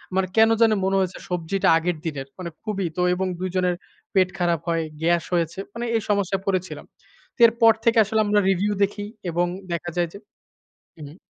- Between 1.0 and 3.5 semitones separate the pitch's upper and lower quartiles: Yes, average, 3.0 semitones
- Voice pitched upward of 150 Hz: Yes, medium, 185 Hz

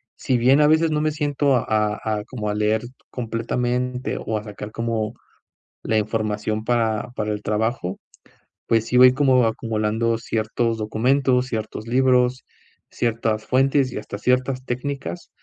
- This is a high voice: No, low, 115 Hz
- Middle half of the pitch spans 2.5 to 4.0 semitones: Yes, average, 2.9 semitones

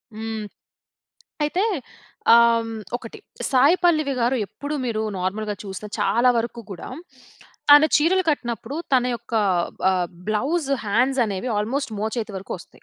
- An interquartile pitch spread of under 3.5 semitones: No, average, 4.6 semitones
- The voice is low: No, high, 235 Hz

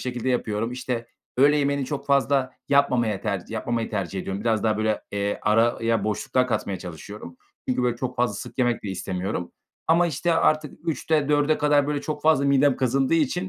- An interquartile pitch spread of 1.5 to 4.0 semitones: No, average, 4.8 semitones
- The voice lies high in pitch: No, low, 125 Hz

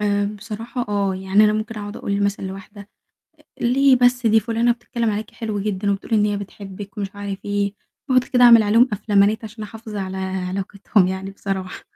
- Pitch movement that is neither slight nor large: No, narrow, 2.2 semitones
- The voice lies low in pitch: No, high, 205 Hz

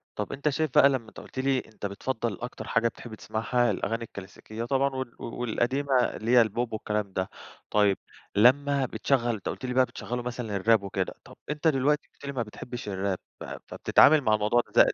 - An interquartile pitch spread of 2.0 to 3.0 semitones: No, average, 3.7 semitones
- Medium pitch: No, low, 120 Hz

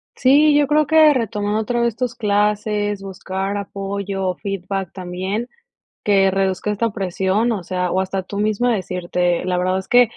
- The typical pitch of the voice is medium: No, high, 200 Hz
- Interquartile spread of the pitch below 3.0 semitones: No, average, 3.3 semitones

